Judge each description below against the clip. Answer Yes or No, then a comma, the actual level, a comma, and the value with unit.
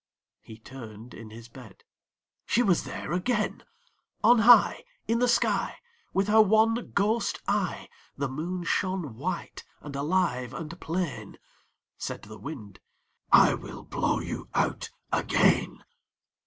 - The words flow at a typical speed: No, slow, 130 wpm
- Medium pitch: Yes, medium, 170 Hz